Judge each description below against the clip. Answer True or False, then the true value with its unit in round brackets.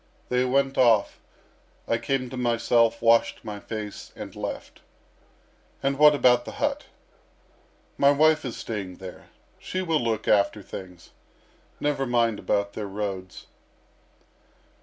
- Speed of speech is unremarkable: False (130 wpm)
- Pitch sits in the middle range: False (115 Hz)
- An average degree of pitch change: True (4.6 semitones)